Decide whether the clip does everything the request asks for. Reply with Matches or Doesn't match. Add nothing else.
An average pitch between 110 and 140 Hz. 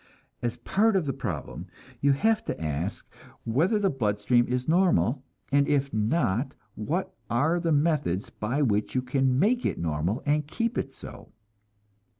Matches